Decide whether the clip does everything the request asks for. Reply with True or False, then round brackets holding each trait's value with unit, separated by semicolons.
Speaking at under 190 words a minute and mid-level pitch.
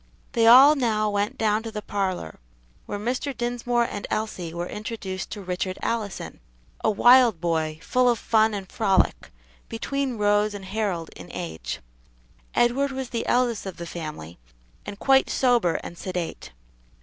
False (155 wpm; 210 Hz)